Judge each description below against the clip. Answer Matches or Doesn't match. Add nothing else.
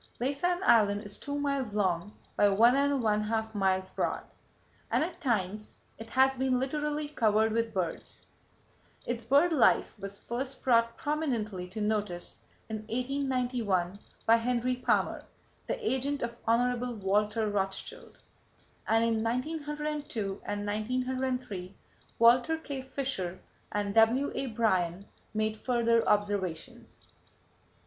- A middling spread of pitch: Matches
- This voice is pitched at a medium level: Doesn't match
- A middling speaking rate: Doesn't match